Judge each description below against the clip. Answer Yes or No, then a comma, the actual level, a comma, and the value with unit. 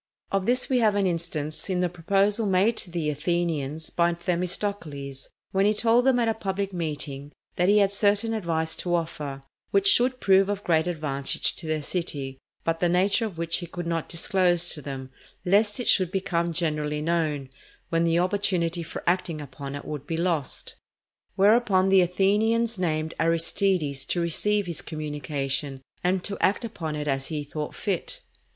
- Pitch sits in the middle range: Yes, medium, 175 Hz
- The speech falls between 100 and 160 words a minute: No, average, 175 wpm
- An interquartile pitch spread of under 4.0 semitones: No, average, 4.4 semitones